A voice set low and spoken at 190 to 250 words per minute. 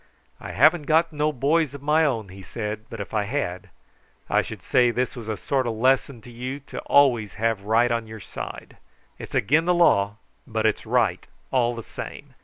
Yes: low, 120 Hz; fast, 205 wpm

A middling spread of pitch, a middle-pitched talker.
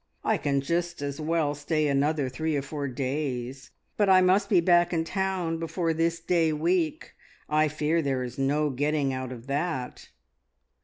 Yes: average, 3.3 semitones; medium, 155 Hz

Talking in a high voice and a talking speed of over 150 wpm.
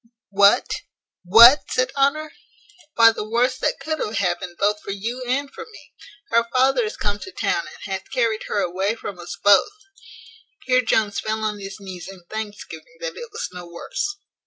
Yes: high, 220 Hz; average, 185 wpm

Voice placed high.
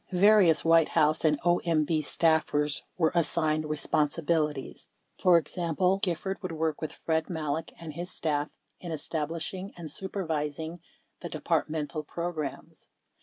No: medium, 160 Hz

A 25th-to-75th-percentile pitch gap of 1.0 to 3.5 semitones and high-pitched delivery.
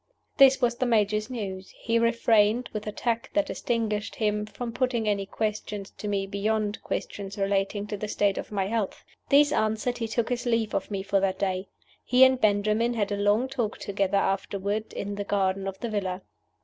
Yes: narrow, 2.6 semitones; high, 210 Hz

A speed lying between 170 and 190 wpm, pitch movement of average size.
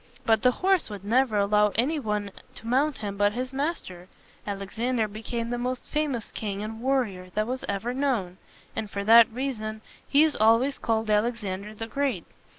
Yes: average, 175 wpm; average, 3.6 semitones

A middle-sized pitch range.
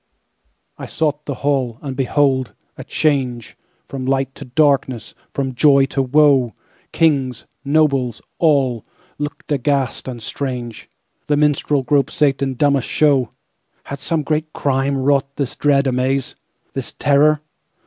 No: narrow, 2.0 semitones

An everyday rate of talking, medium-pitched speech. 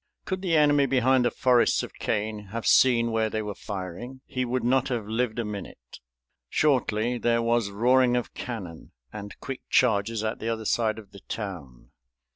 No: average, 180 wpm; low, 115 Hz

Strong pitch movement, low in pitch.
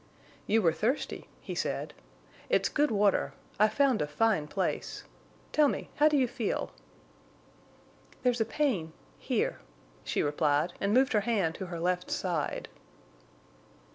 No: wide, 6.7 semitones; high, 210 Hz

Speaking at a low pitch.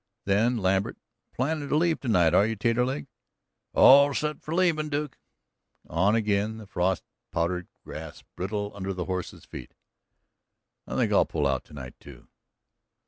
Yes: low, 105 Hz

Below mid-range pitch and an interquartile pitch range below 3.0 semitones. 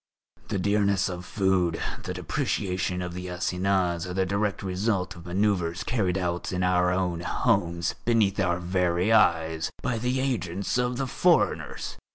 Yes: very low, 90 Hz; narrow, 2.4 semitones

